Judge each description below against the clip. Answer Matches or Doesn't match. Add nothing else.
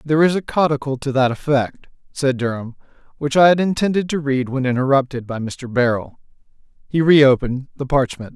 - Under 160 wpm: Doesn't match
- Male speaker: Matches